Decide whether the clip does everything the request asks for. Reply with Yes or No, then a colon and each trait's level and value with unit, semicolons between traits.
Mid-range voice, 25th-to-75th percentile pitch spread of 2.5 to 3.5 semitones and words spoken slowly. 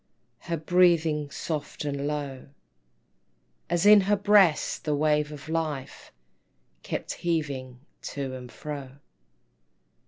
Yes: medium, 150 Hz; average, 3.1 semitones; slow, 105 wpm